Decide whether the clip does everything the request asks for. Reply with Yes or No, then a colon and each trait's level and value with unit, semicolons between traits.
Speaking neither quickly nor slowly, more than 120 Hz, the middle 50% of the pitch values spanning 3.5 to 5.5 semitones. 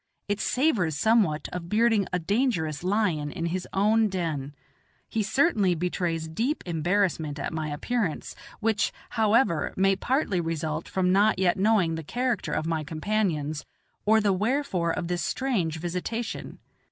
Yes: average, 145 wpm; medium, 185 Hz; average, 5.2 semitones